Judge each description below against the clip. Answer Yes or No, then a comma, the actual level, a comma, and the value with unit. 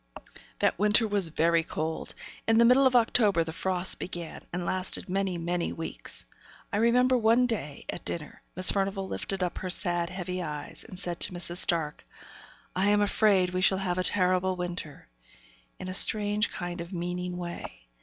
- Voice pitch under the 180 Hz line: No, medium, 185 Hz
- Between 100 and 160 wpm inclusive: No, average, 175 wpm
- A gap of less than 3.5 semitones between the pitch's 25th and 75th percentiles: Yes, average, 2.8 semitones